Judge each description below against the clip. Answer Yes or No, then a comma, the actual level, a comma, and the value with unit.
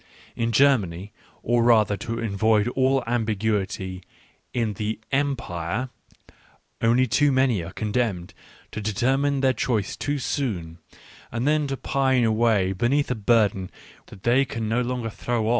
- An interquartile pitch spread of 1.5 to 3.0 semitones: No, average, 3.8 semitones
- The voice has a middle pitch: No, low, 115 Hz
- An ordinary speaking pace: Yes, average, 145 wpm